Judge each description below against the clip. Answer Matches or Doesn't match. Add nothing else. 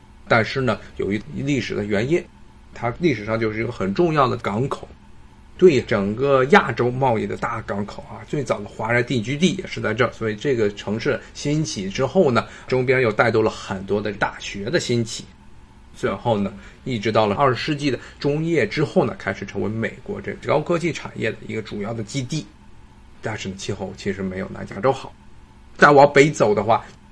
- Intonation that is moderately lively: Matches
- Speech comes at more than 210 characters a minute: Matches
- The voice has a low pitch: Matches